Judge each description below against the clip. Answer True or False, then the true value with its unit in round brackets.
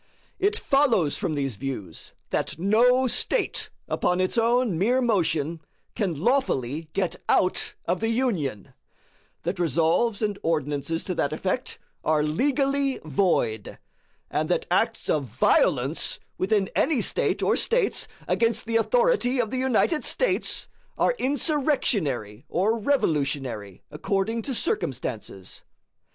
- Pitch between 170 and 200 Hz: True (190 Hz)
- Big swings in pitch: True (8.8 semitones)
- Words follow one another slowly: True (125 wpm)